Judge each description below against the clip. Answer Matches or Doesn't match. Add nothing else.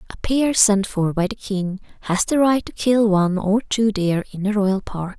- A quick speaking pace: Matches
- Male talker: Doesn't match